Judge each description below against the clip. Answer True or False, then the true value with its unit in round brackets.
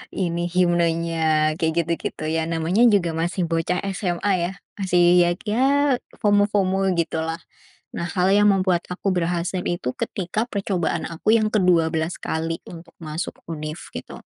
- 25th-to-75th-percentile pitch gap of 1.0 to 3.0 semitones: True (2.6 semitones)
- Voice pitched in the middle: True (175 Hz)